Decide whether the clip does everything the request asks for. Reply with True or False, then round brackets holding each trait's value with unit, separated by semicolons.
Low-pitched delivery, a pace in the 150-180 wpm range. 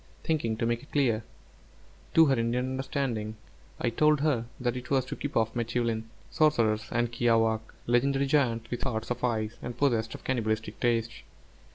True (120 Hz; 170 wpm)